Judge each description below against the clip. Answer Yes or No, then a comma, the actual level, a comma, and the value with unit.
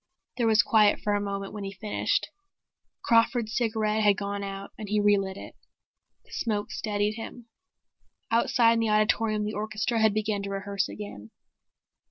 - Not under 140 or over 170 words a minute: Yes, average, 165 wpm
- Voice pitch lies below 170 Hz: No, high, 210 Hz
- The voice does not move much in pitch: Yes, narrow, 1.5 semitones